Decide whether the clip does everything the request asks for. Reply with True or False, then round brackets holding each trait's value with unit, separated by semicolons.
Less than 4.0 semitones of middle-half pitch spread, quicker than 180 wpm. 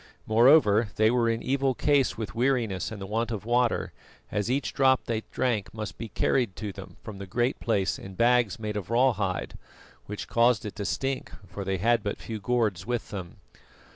True (3.2 semitones; 200 wpm)